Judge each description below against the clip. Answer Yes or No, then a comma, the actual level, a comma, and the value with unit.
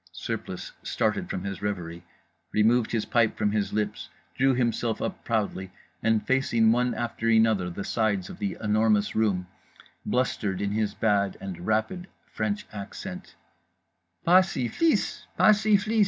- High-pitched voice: No, low, 110 Hz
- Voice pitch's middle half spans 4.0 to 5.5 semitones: No, average, 3.4 semitones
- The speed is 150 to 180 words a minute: No, average, 140 wpm